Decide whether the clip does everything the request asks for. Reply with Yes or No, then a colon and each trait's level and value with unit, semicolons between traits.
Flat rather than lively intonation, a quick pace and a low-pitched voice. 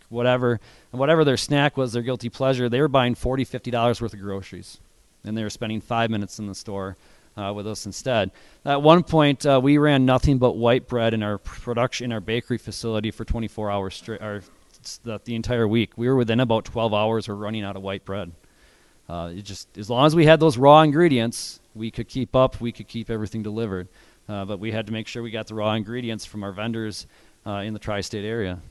No: average, 3.0 semitones; fast, 225 wpm; low, 115 Hz